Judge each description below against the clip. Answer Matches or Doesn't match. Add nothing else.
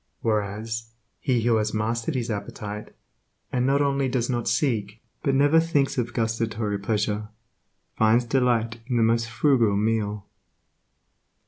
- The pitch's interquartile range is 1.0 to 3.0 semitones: Matches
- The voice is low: Matches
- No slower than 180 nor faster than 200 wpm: Doesn't match